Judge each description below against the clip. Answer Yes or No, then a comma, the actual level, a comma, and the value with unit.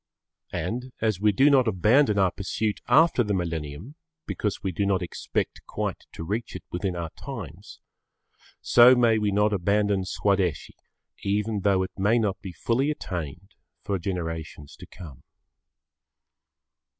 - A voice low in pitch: Yes, low, 100 Hz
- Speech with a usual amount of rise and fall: Yes, average, 3.7 semitones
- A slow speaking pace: No, average, 145 wpm